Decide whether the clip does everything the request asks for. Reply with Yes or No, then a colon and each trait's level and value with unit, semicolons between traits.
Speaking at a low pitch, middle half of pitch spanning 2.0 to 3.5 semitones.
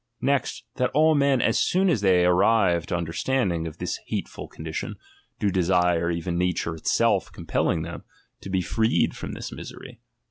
No: very low, 90 Hz; wide, 5.6 semitones